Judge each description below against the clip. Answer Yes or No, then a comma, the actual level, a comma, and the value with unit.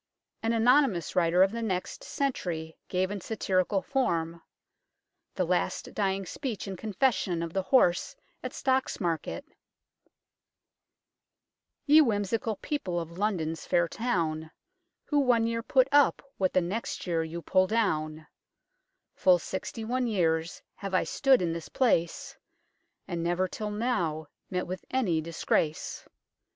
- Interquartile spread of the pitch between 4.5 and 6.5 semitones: Yes, wide, 5.4 semitones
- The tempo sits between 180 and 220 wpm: No, average, 140 wpm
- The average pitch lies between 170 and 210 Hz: Yes, high, 190 Hz